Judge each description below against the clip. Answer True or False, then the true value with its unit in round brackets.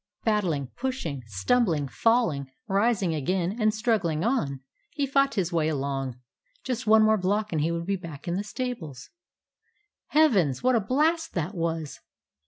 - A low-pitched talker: False (190 Hz)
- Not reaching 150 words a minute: False (155 wpm)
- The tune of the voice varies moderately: False (7.3 semitones)